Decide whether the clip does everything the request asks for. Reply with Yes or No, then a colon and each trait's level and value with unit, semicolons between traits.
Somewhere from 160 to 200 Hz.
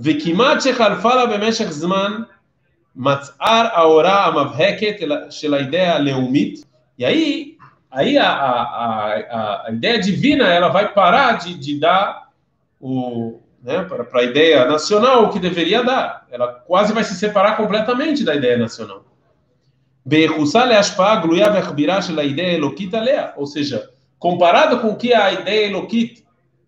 Yes: high, 190 Hz